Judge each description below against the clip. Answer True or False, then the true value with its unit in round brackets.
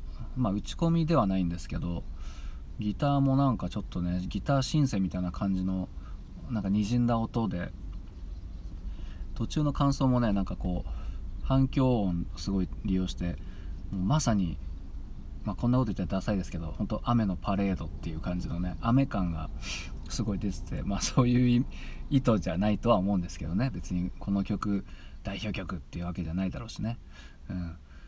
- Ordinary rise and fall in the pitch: True (3.9 semitones)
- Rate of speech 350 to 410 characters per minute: True (355 characters per minute)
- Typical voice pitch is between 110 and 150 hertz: False (95 Hz)